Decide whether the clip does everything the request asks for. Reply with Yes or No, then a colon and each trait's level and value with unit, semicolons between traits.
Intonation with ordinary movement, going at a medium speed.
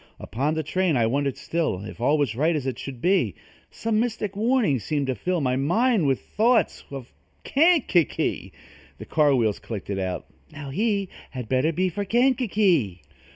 No: wide, 7.9 semitones; average, 175 wpm